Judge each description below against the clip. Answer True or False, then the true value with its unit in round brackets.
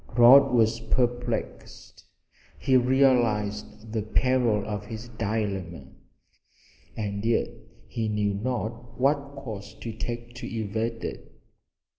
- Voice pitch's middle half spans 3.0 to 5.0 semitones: False (2.5 semitones)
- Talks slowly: True (110 wpm)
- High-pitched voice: False (115 Hz)